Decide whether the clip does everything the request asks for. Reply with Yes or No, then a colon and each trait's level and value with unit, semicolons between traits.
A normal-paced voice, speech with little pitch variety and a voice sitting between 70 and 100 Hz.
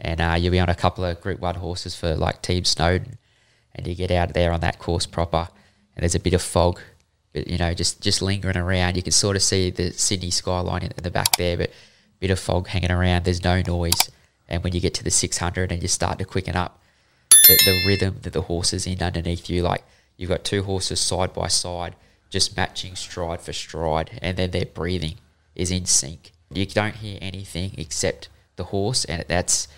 No: fast, 225 wpm; narrow, 1.7 semitones; very low, 90 Hz